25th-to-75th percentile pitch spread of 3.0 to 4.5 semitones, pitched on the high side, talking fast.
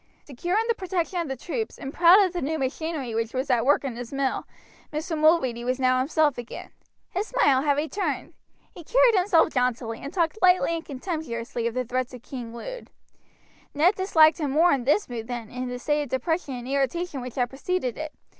No: average, 5.3 semitones; very high, 285 Hz; fast, 210 wpm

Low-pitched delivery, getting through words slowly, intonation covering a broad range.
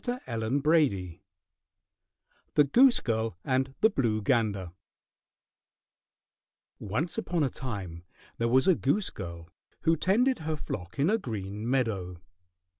Yes: low, 125 Hz; slow, 120 wpm; wide, 7.7 semitones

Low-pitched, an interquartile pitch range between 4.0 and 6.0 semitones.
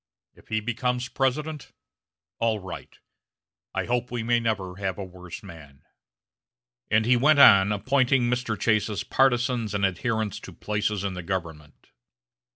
Yes: low, 110 Hz; average, 4.3 semitones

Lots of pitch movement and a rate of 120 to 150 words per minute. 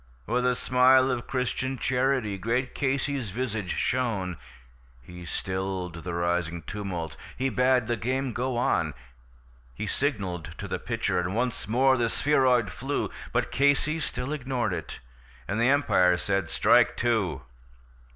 Yes: wide, 5.7 semitones; average, 140 wpm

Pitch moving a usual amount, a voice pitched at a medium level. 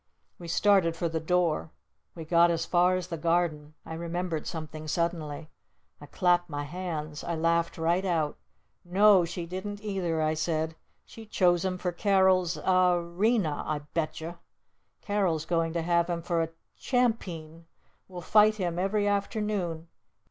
No: narrow, 2.3 semitones; medium, 170 Hz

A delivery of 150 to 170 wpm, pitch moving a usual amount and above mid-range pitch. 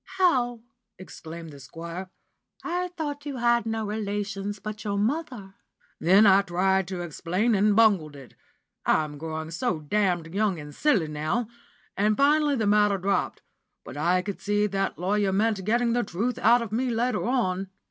Yes: average, 165 wpm; average, 4.5 semitones; high, 205 Hz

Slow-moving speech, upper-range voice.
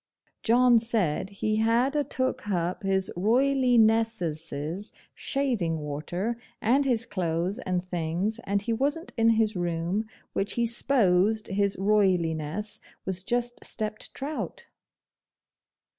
Yes: slow, 115 wpm; high, 210 Hz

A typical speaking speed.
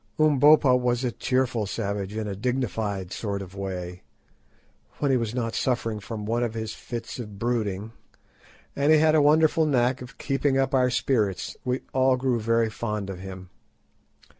Yes: average, 170 wpm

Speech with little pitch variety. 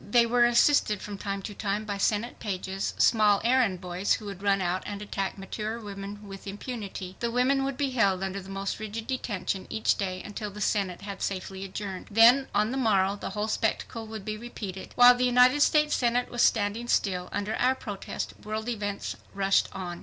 No: average, 3.2 semitones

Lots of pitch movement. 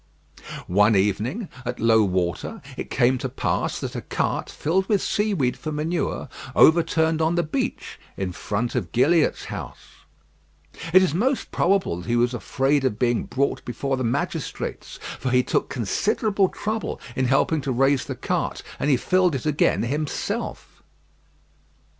Yes: wide, 6.0 semitones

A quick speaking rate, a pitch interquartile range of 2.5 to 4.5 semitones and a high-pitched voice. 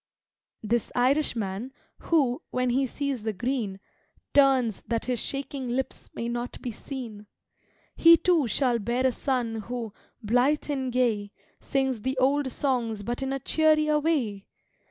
No: average, 145 wpm; average, 3.0 semitones; very high, 255 Hz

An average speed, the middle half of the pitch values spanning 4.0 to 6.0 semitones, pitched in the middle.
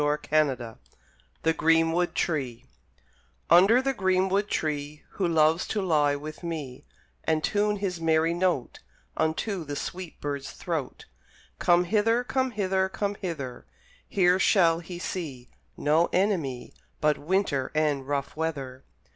No: slow, 130 wpm; average, 4.3 semitones; medium, 165 Hz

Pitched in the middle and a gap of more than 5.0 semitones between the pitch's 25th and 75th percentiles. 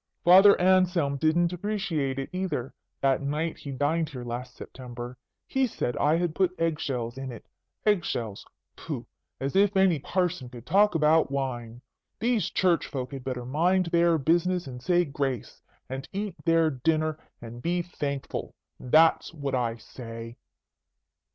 Yes: medium, 155 Hz; wide, 5.5 semitones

